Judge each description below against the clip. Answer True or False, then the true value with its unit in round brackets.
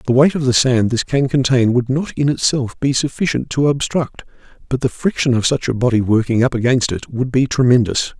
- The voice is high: False (130 Hz)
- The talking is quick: True (220 wpm)